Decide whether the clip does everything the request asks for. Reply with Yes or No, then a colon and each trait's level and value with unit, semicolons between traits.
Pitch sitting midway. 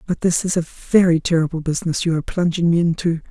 Yes: medium, 170 Hz